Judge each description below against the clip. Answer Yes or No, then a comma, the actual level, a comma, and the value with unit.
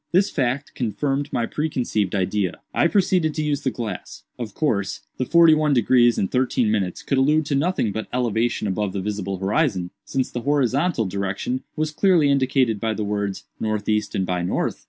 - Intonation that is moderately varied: No, wide, 5.9 semitones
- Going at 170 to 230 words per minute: Yes, average, 180 wpm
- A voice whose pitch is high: No, low, 120 Hz